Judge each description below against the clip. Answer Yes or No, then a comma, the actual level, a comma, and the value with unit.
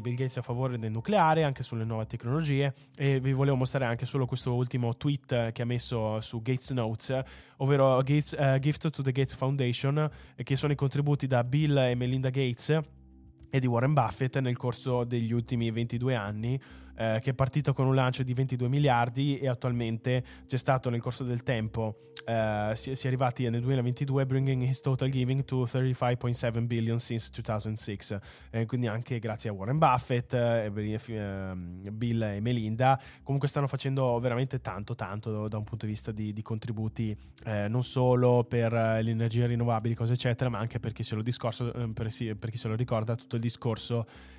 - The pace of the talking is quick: Yes, fast, 185 wpm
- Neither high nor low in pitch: No, low, 125 Hz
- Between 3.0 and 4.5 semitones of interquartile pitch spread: No, narrow, 2.6 semitones